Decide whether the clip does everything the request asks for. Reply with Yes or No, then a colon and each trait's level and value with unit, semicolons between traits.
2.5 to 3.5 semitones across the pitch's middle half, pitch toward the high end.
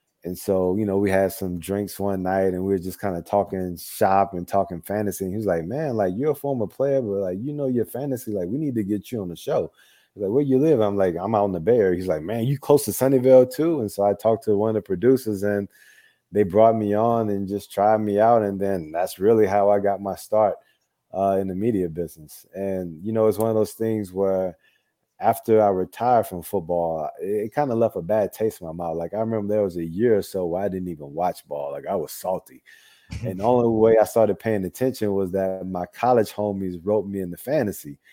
No: average, 2.9 semitones; low, 100 Hz